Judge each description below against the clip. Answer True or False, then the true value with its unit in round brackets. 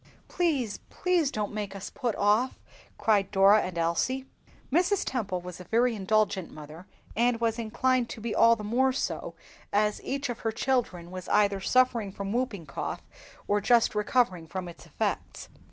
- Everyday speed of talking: True (170 wpm)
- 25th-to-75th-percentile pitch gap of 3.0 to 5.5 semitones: True (4.3 semitones)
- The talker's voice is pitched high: True (215 Hz)